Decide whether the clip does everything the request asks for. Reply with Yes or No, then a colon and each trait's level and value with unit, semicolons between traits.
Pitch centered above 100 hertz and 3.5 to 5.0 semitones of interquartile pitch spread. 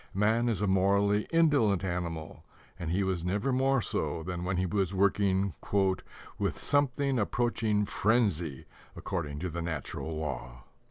No: very low, 95 Hz; average, 4.1 semitones